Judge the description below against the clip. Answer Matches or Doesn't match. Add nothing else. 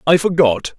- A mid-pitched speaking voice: Matches